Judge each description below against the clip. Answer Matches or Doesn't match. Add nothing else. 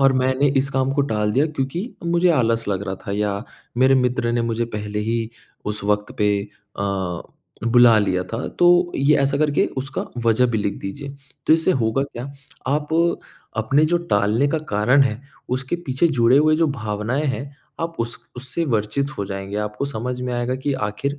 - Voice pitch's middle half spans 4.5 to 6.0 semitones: Matches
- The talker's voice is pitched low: Matches